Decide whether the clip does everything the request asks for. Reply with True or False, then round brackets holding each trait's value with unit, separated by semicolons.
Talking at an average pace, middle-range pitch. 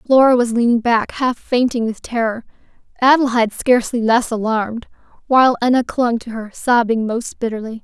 False (155 wpm; 235 Hz)